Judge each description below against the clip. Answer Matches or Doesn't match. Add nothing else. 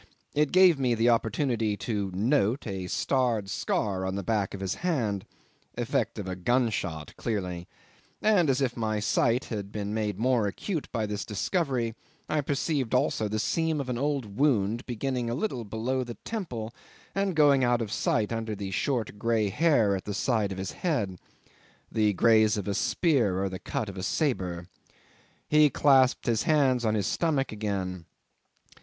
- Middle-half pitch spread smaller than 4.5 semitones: Doesn't match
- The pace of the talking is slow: Doesn't match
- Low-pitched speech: Matches